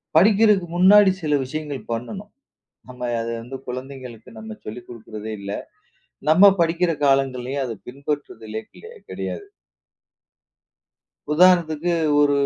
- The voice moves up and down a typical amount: No, wide, 6.2 semitones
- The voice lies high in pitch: No, medium, 140 Hz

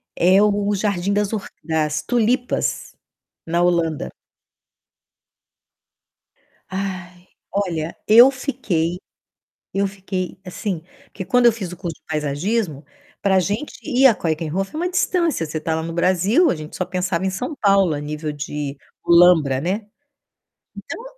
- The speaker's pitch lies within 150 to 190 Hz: Yes, medium, 185 Hz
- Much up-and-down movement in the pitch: No, average, 4.2 semitones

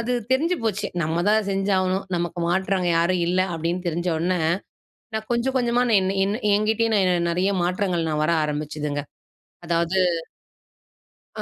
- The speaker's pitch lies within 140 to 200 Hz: Yes, medium, 185 Hz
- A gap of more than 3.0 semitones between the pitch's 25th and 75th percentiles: Yes, average, 3.6 semitones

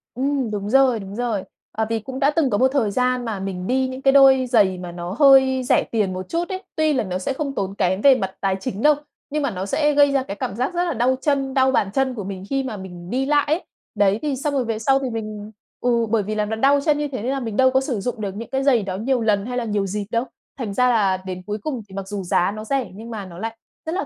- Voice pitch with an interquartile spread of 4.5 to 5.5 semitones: Yes, average, 5.0 semitones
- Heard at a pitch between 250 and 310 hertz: No, high, 235 Hz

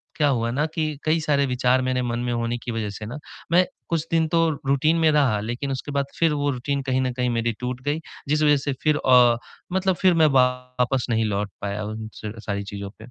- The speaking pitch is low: Yes, low, 130 Hz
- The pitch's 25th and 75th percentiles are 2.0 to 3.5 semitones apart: No, average, 4.1 semitones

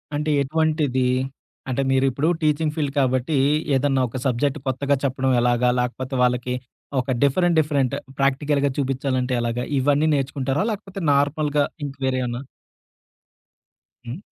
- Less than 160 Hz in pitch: Yes, low, 135 Hz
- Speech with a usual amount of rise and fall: No, narrow, 2.3 semitones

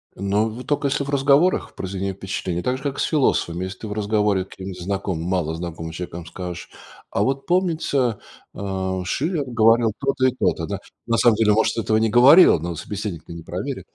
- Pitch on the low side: Yes, low, 105 Hz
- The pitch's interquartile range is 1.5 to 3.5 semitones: No, wide, 5.9 semitones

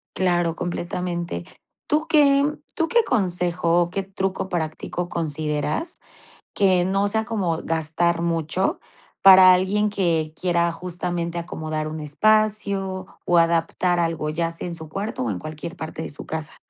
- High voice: No, medium, 175 Hz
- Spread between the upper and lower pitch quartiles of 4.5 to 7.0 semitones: No, average, 2.9 semitones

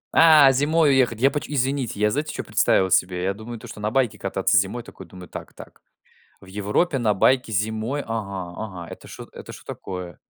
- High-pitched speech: No, low, 110 Hz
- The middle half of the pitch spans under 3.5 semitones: No, wide, 5.7 semitones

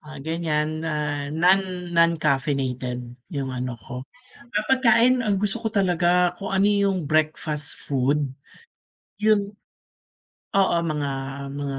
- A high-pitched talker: No, medium, 160 Hz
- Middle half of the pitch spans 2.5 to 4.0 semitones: No, average, 5.3 semitones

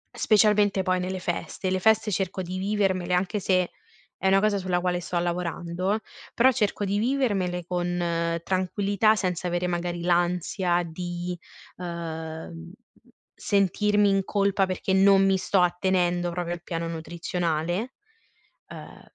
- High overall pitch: No, medium, 180 Hz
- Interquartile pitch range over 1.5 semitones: Yes, narrow, 2.2 semitones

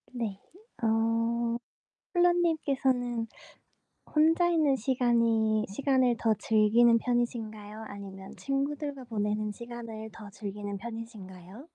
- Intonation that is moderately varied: Yes, average, 3.4 semitones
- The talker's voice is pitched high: Yes, high, 230 Hz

